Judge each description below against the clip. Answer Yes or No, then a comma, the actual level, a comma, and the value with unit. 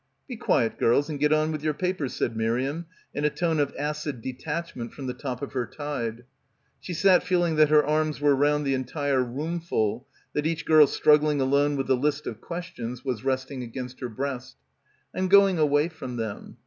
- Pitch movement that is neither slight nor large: Yes, average, 3.3 semitones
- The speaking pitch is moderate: Yes, medium, 145 Hz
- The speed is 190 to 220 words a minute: Yes, average, 195 wpm